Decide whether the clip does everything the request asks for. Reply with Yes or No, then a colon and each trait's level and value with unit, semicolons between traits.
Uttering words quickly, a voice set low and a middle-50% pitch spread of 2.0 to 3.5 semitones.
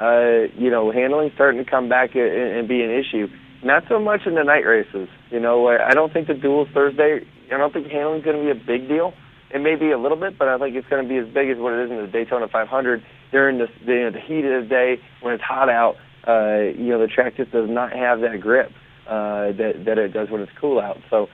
Yes: fast, 270 wpm; low, 130 Hz; average, 2.9 semitones